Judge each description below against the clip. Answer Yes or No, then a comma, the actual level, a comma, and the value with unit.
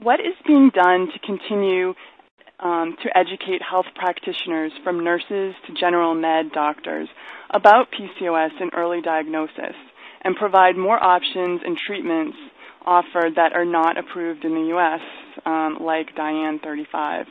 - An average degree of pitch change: Yes, average, 3.3 semitones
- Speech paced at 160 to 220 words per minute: No, average, 140 wpm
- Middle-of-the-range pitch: Yes, medium, 180 Hz